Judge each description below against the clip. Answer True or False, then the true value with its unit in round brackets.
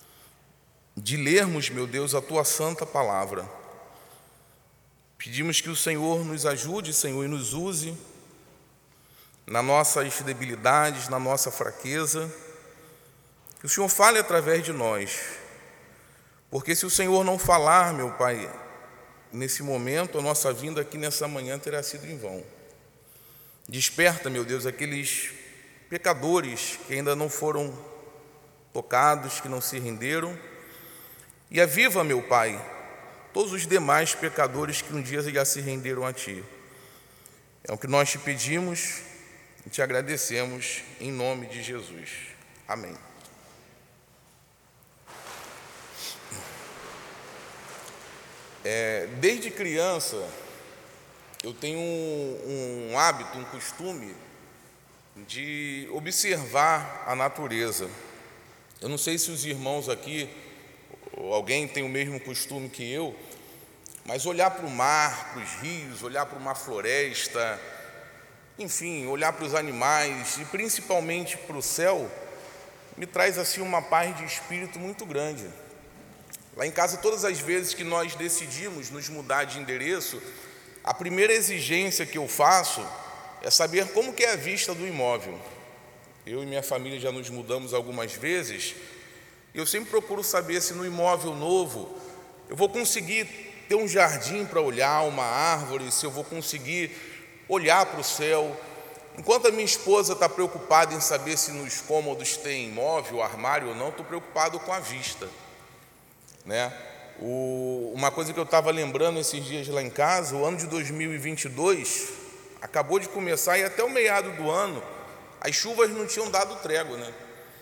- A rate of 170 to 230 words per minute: False (140 wpm)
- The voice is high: False (150 Hz)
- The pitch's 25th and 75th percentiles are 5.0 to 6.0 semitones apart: False (4.5 semitones)